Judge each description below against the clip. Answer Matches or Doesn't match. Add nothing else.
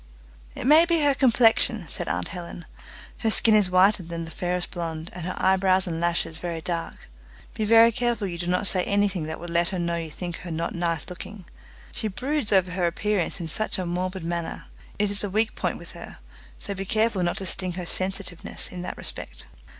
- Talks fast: Matches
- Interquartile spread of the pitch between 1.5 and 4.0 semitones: Matches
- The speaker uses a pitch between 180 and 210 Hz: Matches